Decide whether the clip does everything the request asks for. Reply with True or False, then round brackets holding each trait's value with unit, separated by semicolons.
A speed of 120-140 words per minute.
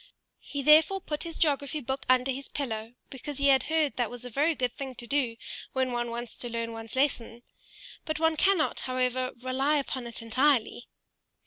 False (190 wpm)